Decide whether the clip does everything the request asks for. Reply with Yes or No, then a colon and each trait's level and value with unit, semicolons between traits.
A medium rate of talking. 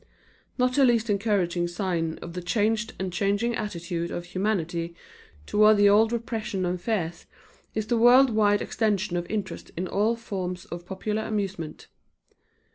Yes: average, 150 wpm